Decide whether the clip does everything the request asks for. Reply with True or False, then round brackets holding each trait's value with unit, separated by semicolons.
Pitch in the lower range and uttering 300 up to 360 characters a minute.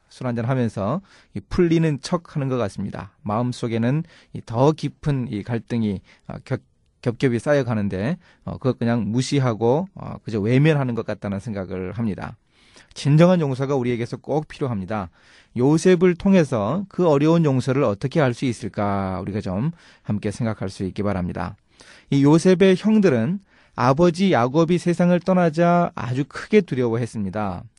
True (125 Hz; 315 characters per minute)